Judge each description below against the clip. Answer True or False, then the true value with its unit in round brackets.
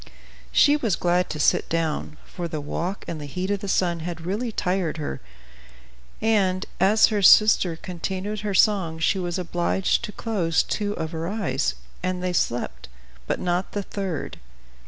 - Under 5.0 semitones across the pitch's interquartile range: True (3.4 semitones)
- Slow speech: False (170 wpm)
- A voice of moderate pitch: True (180 Hz)